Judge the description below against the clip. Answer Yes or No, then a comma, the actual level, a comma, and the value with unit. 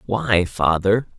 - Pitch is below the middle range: Yes, low, 100 Hz